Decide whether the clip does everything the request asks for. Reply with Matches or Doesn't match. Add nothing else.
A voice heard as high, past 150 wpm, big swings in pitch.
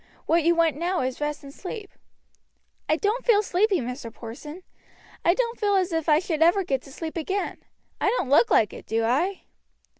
Matches